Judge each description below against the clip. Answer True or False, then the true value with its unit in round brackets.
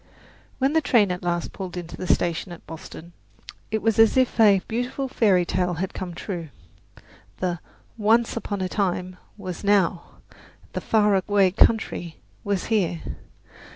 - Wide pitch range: False (3.7 semitones)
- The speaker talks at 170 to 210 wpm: False (155 wpm)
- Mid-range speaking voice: False (195 Hz)